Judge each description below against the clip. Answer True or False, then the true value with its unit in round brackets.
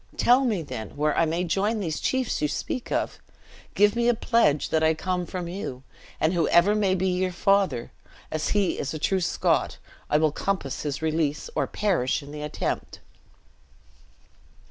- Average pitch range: True (4.8 semitones)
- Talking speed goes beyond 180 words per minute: False (175 wpm)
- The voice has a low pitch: False (175 Hz)